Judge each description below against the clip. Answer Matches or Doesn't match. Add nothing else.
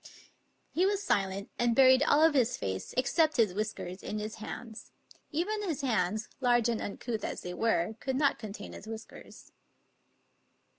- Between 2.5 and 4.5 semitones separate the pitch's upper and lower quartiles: Doesn't match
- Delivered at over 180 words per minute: Doesn't match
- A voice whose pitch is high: Matches